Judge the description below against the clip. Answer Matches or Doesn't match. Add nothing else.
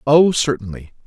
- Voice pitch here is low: Matches